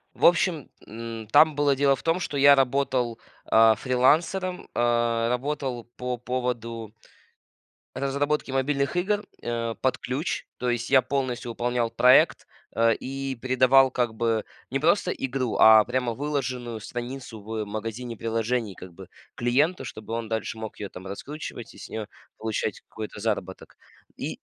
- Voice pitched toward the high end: No, low, 125 Hz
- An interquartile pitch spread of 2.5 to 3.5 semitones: Yes, average, 3.2 semitones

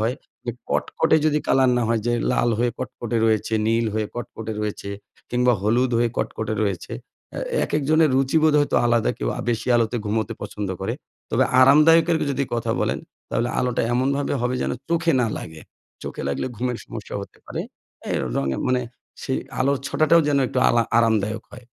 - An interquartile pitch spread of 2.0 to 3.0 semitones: No, average, 3.5 semitones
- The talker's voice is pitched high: No, low, 120 Hz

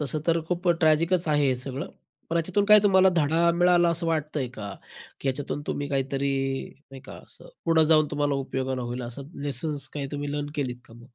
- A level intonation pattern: No, average, 3.6 semitones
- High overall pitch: No, medium, 145 Hz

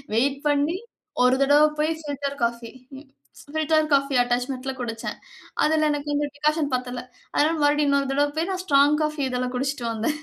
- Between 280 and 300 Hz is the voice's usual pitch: Yes, very high, 285 Hz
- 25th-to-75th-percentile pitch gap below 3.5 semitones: Yes, average, 2.9 semitones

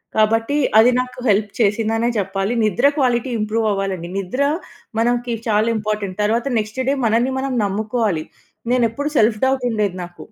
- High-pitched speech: Yes, high, 220 Hz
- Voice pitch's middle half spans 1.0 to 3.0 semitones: Yes, average, 2.7 semitones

